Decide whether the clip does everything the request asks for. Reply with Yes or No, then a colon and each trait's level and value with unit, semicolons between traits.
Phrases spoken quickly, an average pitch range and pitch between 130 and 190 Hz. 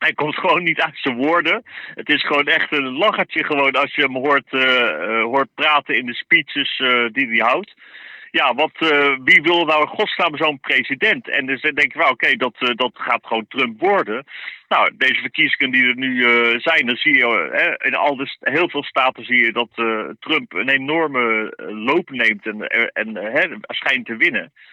Yes: fast, 215 wpm; average, 3.6 semitones; medium, 140 Hz